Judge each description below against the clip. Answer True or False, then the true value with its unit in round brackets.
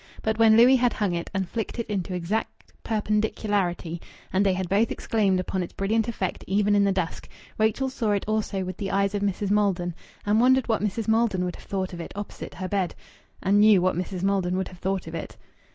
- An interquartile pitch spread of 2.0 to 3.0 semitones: True (2.7 semitones)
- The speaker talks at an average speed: False (220 wpm)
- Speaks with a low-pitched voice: False (200 Hz)